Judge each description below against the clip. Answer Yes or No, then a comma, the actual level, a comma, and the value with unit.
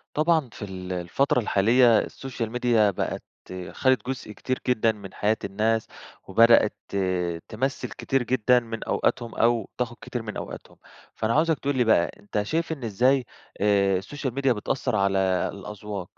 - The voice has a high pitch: No, low, 115 Hz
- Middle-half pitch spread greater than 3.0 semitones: Yes, average, 3.8 semitones